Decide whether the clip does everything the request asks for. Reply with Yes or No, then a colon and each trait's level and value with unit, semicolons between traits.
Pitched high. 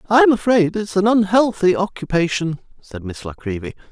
No: medium, 175 Hz